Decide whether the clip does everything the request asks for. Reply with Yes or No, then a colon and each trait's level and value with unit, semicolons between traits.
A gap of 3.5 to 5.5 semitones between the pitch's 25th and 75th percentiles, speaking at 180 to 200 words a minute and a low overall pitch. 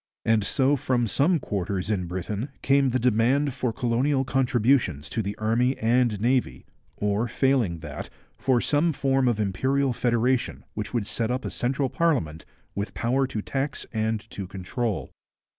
No: average, 4.2 semitones; average, 160 wpm; low, 120 Hz